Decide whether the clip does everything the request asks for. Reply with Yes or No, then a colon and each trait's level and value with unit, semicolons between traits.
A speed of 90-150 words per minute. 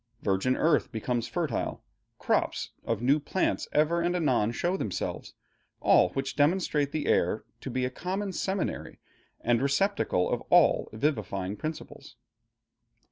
Yes: slow, 135 wpm